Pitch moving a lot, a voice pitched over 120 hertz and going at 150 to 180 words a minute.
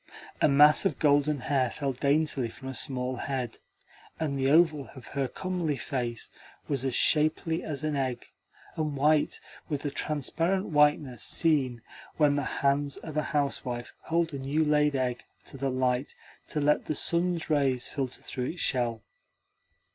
No: average, 2.8 semitones; medium, 140 Hz; average, 160 wpm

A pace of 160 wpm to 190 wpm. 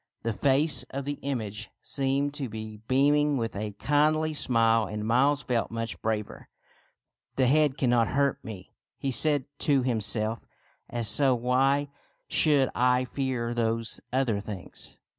No: average, 150 wpm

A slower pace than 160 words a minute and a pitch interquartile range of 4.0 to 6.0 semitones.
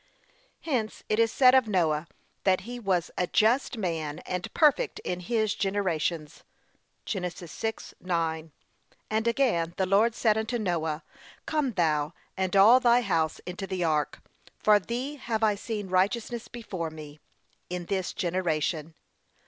Yes: average, 140 wpm; average, 4.9 semitones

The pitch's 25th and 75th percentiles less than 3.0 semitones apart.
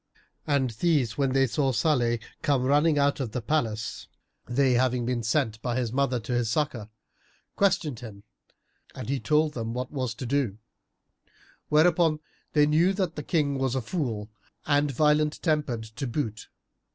No: average, 4.1 semitones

